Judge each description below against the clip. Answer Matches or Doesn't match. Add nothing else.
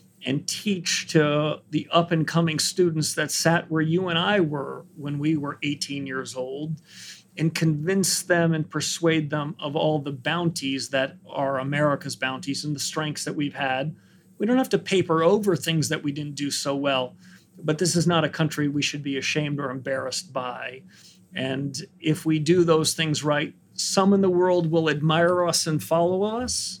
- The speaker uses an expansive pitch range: Doesn't match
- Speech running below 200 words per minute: Matches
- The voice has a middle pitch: Matches